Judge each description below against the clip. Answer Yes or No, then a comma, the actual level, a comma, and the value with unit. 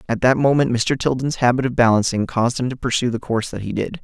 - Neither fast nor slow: No, fast, 255 wpm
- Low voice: Yes, low, 125 Hz